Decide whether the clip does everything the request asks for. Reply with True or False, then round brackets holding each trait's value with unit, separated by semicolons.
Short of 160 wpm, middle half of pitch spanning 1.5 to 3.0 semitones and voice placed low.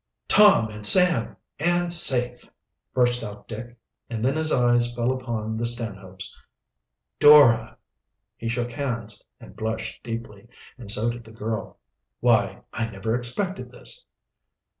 True (135 wpm; 2.4 semitones; 120 Hz)